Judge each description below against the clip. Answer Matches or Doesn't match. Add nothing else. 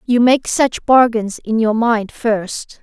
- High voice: Matches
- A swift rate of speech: Doesn't match